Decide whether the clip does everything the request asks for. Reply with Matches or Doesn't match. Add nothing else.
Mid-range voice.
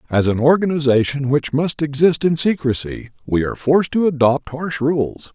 Matches